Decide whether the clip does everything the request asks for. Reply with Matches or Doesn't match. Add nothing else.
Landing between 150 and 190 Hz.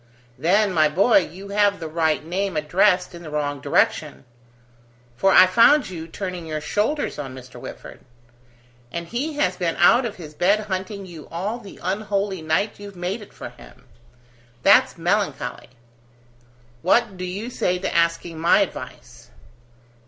Matches